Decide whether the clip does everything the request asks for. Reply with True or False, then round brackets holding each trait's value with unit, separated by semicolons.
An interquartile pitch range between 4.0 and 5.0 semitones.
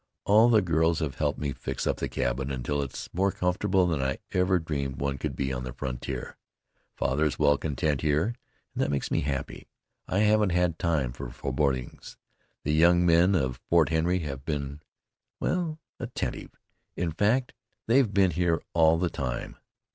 True (4.7 semitones)